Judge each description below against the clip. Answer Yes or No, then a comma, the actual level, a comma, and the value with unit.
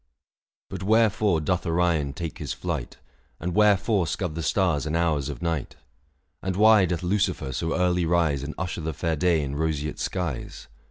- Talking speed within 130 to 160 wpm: No, average, 175 wpm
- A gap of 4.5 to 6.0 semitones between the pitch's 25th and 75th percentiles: No, average, 3.3 semitones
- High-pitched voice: No, very low, 85 Hz